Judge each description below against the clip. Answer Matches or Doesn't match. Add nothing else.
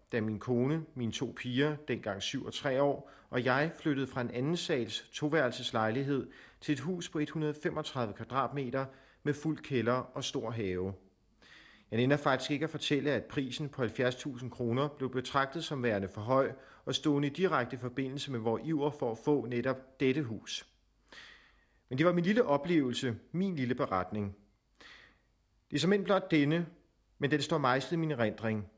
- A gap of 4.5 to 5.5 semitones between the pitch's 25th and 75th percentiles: Doesn't match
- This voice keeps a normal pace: Matches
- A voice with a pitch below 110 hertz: Doesn't match